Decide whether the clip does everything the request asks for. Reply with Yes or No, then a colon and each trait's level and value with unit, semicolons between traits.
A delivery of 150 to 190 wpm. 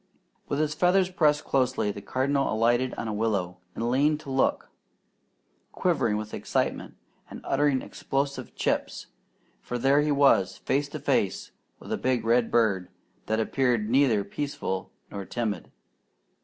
No: average, 140 wpm